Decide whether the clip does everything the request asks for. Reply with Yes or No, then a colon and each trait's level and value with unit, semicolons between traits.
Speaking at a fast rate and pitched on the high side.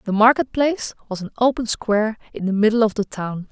Yes: fast, 220 wpm; high, 220 Hz